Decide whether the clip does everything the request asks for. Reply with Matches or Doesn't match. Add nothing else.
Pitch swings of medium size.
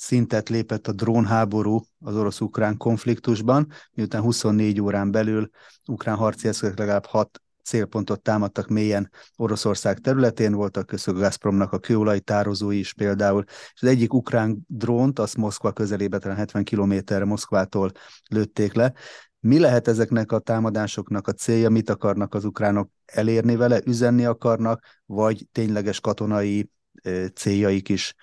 Doesn't match